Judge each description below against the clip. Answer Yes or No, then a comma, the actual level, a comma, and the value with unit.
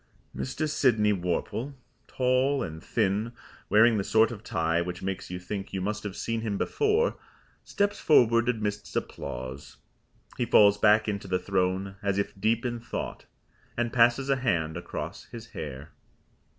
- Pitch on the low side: Yes, low, 105 Hz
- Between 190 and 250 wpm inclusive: No, average, 155 wpm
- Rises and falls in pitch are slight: No, average, 4.2 semitones